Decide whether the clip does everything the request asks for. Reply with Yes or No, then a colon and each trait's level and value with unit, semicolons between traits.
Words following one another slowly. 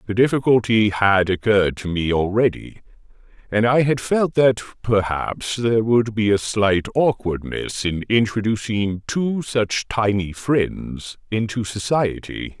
Yes: slow, 130 wpm